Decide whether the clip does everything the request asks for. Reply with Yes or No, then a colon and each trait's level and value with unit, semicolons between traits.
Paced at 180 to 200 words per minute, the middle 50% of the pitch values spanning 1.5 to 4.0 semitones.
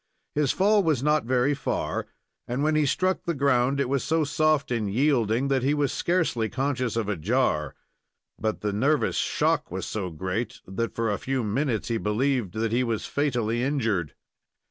No: average, 185 wpm; average, 4.5 semitones